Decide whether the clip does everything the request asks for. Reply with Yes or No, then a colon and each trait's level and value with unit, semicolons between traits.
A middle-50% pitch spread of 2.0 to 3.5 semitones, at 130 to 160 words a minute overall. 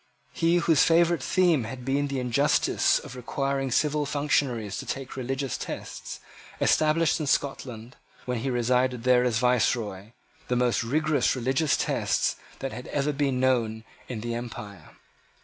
Yes: average, 3.0 semitones; average, 150 wpm